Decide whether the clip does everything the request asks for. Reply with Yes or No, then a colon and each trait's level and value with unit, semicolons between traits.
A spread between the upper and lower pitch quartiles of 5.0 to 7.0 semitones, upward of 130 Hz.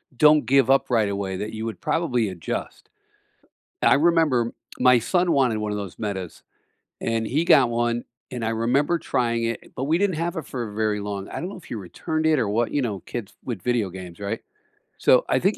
No: wide, 5.4 semitones; low, 120 Hz